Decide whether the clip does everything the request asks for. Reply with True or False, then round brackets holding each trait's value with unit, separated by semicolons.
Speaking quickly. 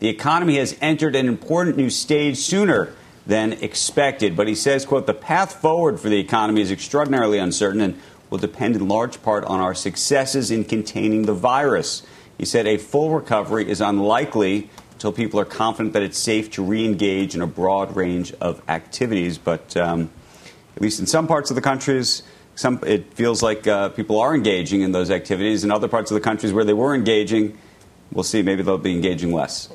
False (195 wpm)